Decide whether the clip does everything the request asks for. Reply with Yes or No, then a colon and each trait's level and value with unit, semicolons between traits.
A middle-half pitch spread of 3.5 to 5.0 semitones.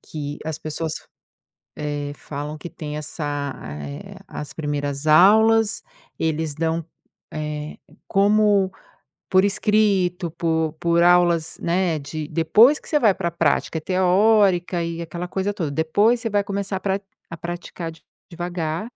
Yes: average, 4.0 semitones